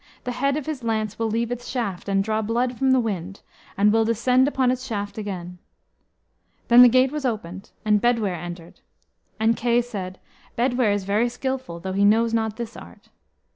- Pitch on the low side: No, high, 225 Hz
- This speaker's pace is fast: No, average, 190 wpm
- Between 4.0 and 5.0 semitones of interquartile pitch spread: No, average, 3.4 semitones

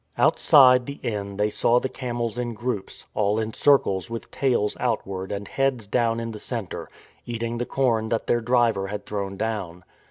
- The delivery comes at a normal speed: Yes, average, 180 wpm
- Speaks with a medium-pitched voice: No, low, 115 Hz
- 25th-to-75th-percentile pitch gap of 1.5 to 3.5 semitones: Yes, average, 3.0 semitones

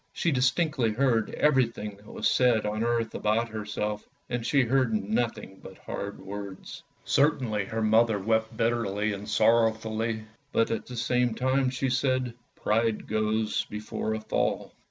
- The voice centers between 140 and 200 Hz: No, low, 110 Hz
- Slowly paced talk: No, average, 155 wpm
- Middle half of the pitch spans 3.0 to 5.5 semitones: No, narrow, 2.5 semitones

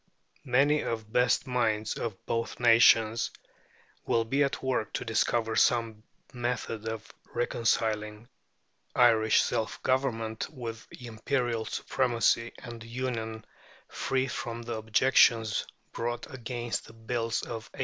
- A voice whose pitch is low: Yes, low, 115 Hz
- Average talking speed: No, slow, 120 wpm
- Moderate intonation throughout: No, narrow, 1.7 semitones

